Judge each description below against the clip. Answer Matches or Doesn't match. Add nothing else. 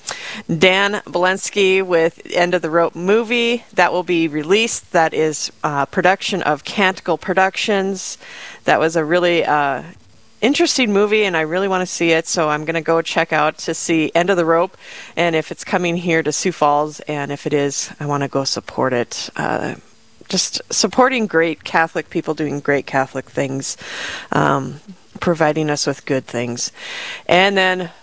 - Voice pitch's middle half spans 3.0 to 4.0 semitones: Matches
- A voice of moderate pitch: Matches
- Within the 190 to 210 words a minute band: Doesn't match